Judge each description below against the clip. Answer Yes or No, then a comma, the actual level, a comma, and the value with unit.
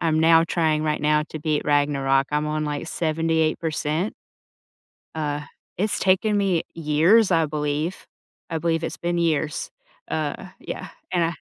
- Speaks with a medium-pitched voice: Yes, medium, 160 Hz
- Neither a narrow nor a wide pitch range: No, narrow, 1.9 semitones